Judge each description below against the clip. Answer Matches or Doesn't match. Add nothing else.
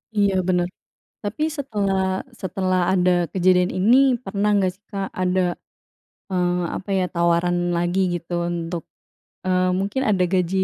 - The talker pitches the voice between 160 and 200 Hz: Matches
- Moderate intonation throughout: Doesn't match